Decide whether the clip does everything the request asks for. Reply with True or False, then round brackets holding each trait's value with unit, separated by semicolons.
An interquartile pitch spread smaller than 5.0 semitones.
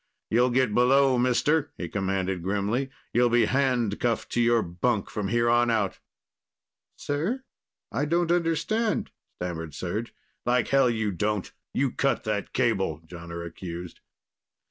False (5.3 semitones)